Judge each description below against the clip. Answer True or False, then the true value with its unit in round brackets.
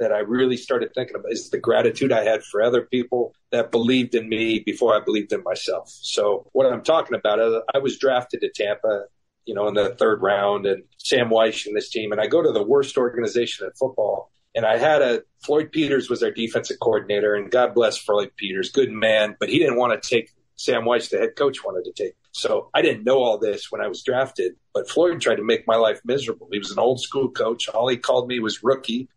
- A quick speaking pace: True (240 wpm)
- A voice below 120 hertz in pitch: False (135 Hz)